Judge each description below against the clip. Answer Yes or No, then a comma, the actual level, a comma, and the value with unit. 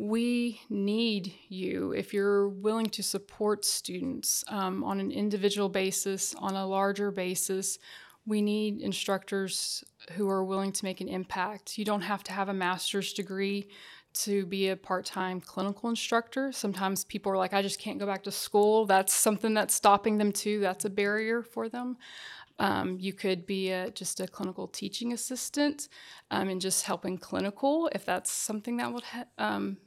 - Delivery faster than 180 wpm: No, average, 175 wpm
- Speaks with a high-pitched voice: Yes, high, 200 Hz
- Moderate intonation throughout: No, narrow, 2.0 semitones